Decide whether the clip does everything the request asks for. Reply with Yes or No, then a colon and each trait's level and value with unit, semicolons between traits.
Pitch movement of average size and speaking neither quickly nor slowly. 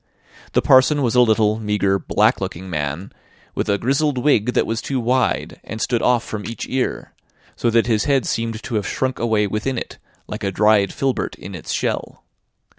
Yes: average, 3.4 semitones; average, 190 wpm